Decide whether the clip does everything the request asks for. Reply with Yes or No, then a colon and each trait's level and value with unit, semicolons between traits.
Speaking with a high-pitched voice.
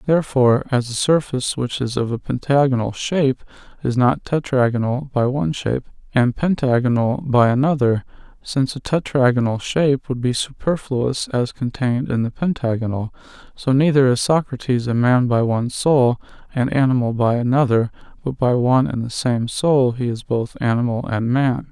No: low, 130 Hz